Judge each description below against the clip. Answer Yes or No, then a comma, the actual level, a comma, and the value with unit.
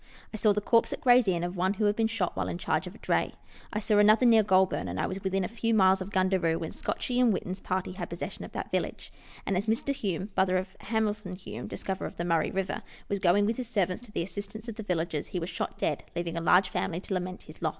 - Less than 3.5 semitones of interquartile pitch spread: Yes, average, 3.0 semitones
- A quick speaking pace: Yes, fast, 270 wpm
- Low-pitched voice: No, high, 190 Hz